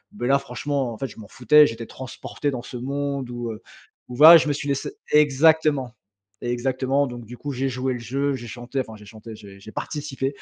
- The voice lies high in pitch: No, low, 130 Hz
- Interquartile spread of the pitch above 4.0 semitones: No, average, 2.9 semitones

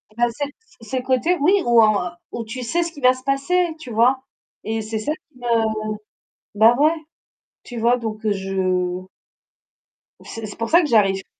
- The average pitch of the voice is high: Yes, high, 235 Hz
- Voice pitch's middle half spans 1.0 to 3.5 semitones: No, average, 4.0 semitones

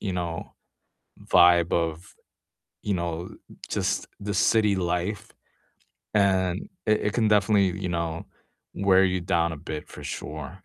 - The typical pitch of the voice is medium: No, very low, 90 Hz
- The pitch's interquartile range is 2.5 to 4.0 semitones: Yes, average, 2.8 semitones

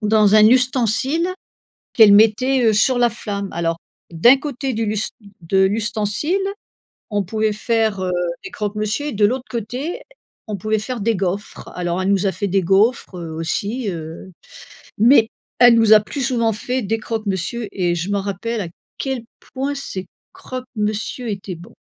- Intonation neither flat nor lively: Yes, average, 3.6 semitones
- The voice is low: No, high, 215 Hz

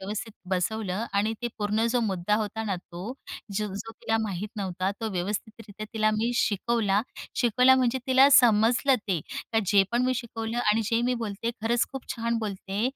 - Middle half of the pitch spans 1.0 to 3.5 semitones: Yes, average, 2.7 semitones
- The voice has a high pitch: Yes, high, 220 Hz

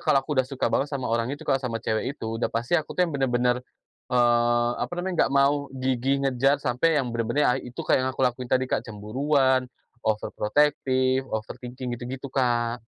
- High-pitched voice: No, low, 130 Hz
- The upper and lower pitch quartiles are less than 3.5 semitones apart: Yes, narrow, 2.5 semitones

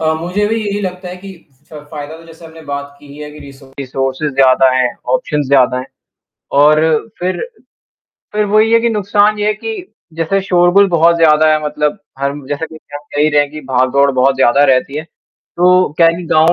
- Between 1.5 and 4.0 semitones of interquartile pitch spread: No, average, 4.4 semitones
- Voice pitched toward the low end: No, medium, 155 Hz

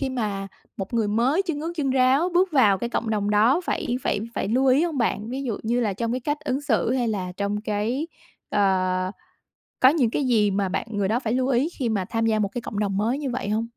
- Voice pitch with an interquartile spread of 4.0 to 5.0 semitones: Yes, average, 4.3 semitones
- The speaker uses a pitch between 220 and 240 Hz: Yes, high, 230 Hz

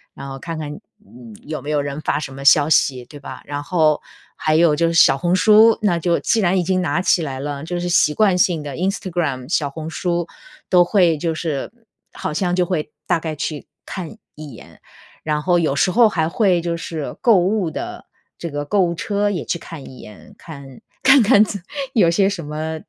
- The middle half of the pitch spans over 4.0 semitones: No, average, 3.6 semitones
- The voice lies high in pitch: No, medium, 165 Hz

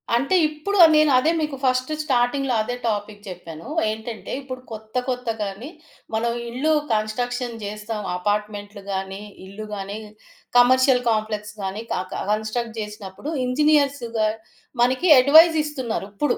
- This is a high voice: Yes, high, 235 Hz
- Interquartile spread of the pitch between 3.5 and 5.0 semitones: Yes, average, 3.9 semitones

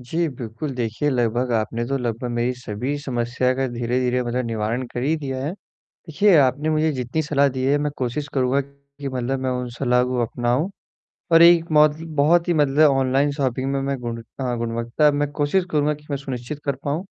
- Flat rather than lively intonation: No, average, 3.1 semitones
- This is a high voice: No, low, 135 Hz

